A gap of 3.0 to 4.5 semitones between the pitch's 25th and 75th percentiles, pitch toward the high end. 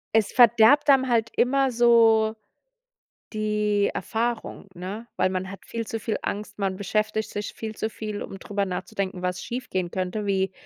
No: narrow, 2.5 semitones; high, 215 Hz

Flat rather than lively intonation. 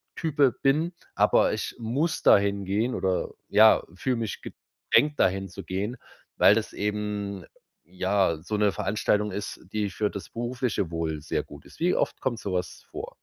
No: average, 3.9 semitones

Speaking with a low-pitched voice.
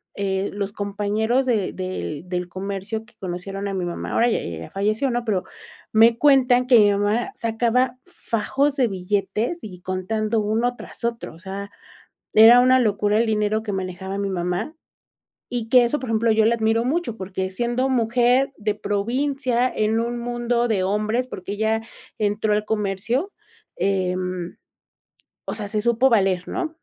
No: high, 220 Hz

